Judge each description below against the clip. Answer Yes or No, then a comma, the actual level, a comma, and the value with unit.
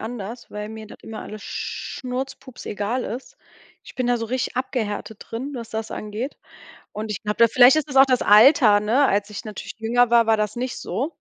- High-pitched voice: Yes, high, 230 Hz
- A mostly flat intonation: No, average, 3.1 semitones